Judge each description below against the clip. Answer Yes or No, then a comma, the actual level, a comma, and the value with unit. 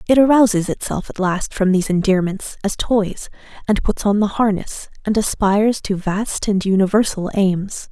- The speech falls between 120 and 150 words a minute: No, average, 165 wpm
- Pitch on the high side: Yes, high, 205 Hz